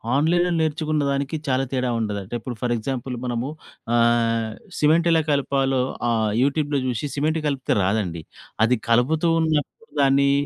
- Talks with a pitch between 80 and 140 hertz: Yes, low, 135 Hz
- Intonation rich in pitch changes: No, average, 4.2 semitones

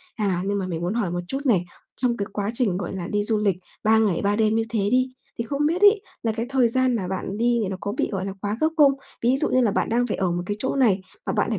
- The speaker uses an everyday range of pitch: Yes, average, 4.1 semitones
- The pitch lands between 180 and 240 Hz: Yes, high, 215 Hz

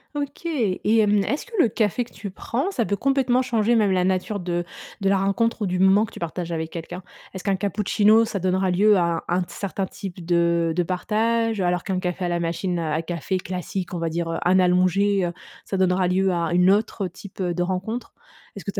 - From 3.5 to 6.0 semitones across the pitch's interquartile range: No, average, 3.0 semitones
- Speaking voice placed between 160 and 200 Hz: Yes, high, 190 Hz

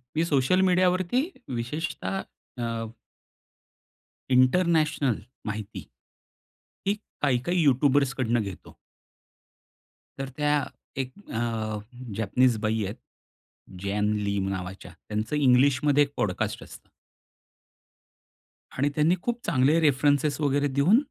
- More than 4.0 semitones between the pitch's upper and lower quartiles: Yes, average, 5.0 semitones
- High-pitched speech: No, low, 135 Hz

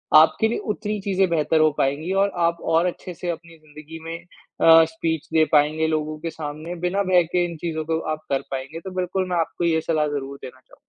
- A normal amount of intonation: No, narrow, 2.2 semitones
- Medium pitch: Yes, medium, 165 Hz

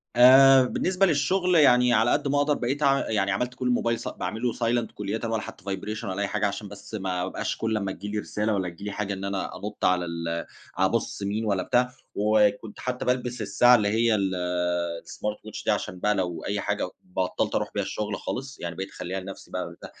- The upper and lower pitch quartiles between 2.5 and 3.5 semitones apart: No, average, 4.1 semitones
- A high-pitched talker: No, low, 105 Hz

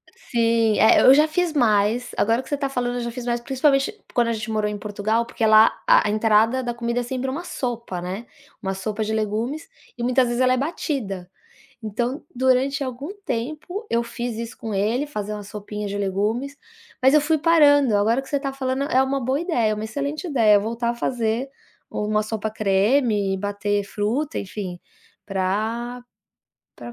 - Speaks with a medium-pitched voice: No, high, 235 Hz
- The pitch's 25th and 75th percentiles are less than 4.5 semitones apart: Yes, average, 4.0 semitones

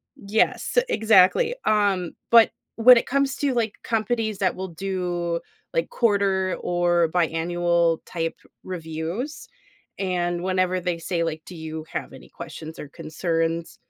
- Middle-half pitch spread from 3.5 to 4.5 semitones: Yes, average, 4.1 semitones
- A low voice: No, medium, 180 Hz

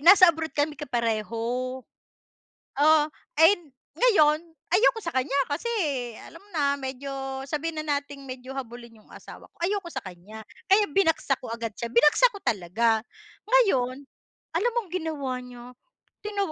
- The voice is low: No, very high, 285 Hz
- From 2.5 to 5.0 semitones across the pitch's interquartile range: No, wide, 5.4 semitones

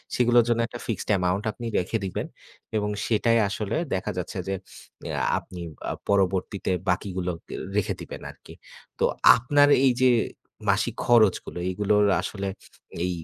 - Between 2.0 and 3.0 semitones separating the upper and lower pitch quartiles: No, average, 3.8 semitones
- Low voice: Yes, low, 105 Hz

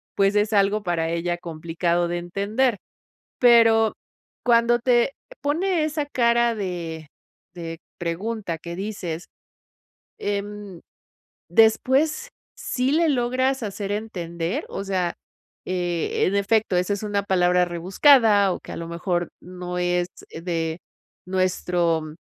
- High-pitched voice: Yes, high, 195 Hz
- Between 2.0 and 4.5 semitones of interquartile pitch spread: No, average, 4.9 semitones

